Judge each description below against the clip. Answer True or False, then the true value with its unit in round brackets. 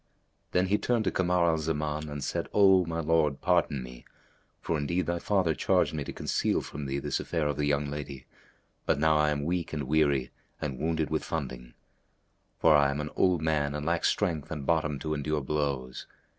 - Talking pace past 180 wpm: True (200 wpm)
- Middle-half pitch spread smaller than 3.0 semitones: True (2.5 semitones)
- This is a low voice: True (75 Hz)